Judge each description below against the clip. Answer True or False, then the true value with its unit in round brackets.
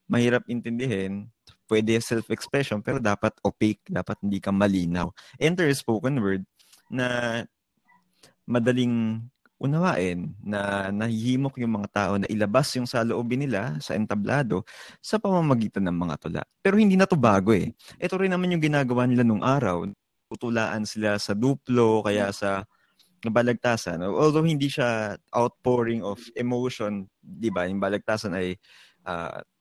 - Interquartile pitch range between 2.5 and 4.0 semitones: True (3.6 semitones)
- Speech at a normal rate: True (140 wpm)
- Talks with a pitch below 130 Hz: True (115 Hz)